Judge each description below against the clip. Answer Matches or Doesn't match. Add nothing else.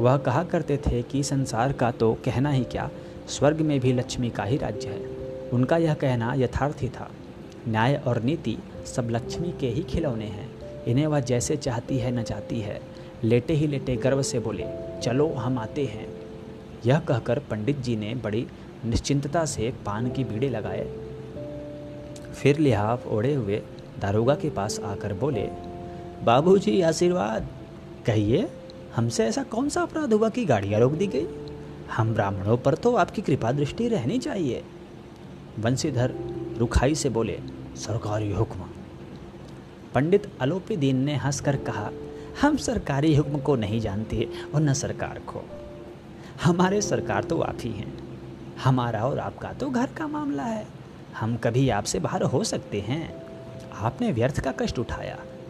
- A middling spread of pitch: Matches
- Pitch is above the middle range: Doesn't match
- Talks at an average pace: Matches